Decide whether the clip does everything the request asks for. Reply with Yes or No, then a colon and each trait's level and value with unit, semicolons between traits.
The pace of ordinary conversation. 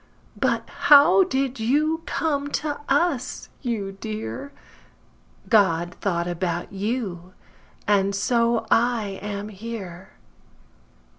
No: slow, 90 wpm